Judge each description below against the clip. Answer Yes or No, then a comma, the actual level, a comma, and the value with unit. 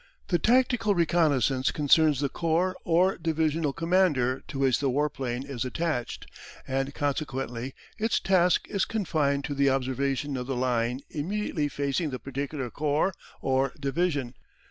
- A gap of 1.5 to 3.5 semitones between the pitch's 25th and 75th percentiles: No, average, 3.9 semitones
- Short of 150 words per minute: Yes, average, 140 wpm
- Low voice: No, medium, 145 Hz